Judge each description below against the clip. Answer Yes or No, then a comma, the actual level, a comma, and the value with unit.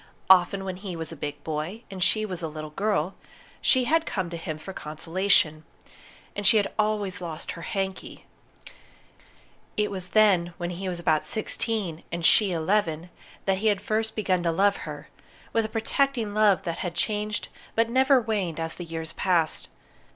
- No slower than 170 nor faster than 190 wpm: Yes, average, 180 wpm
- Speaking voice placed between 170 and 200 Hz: Yes, high, 190 Hz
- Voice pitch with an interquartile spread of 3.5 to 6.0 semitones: Yes, average, 4.1 semitones